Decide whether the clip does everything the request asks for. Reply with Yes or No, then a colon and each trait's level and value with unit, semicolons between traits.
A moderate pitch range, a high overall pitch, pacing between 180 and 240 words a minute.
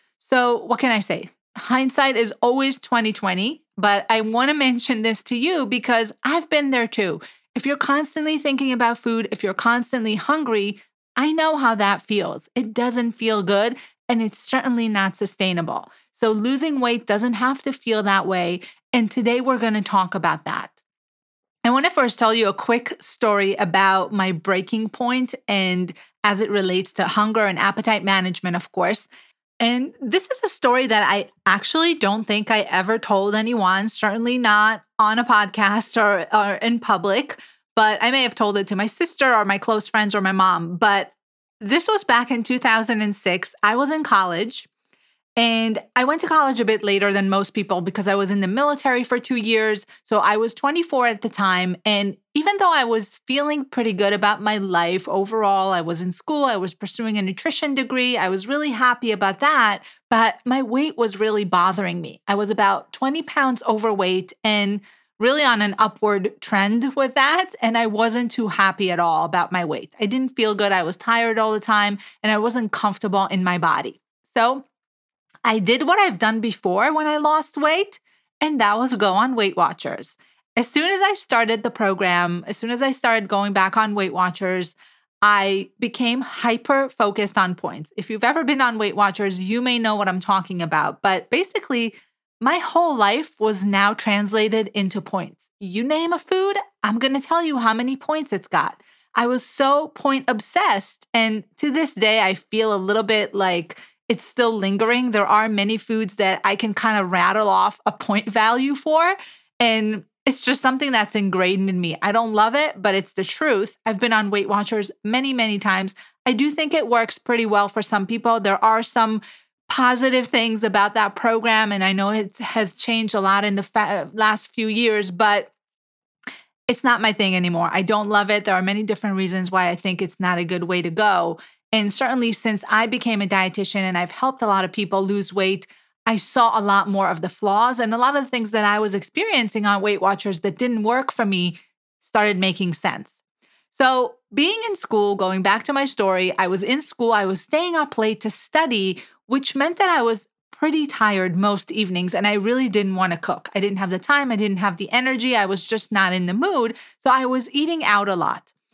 Yes: average, 3.9 semitones; high, 220 Hz; fast, 205 wpm